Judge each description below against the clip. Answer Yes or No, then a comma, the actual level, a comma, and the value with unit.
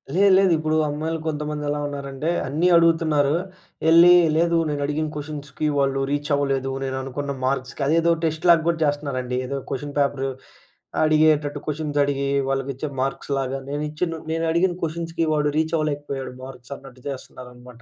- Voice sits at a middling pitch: Yes, medium, 145 Hz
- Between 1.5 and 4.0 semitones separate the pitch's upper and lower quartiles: Yes, narrow, 2.6 semitones